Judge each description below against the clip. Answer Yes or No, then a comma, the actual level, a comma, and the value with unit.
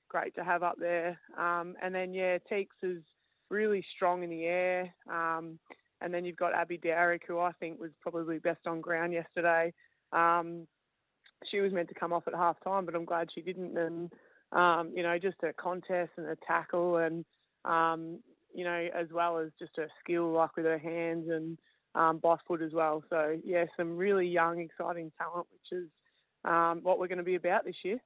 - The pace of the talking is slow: No, fast, 205 wpm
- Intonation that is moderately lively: No, narrow, 1.1 semitones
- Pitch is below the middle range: No, medium, 170 Hz